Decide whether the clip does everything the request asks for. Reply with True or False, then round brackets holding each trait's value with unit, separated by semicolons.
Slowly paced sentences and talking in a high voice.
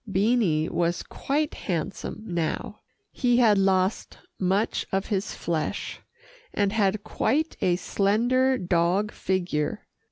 True (115 wpm; 195 Hz)